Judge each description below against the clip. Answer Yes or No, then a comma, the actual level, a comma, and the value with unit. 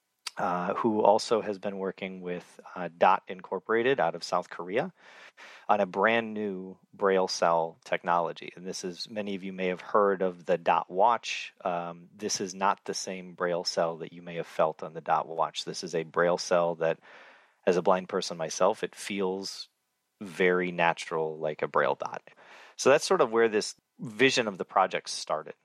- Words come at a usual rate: Yes, average, 190 wpm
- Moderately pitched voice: No, very low, 95 Hz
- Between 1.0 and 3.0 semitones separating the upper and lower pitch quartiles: Yes, average, 2.7 semitones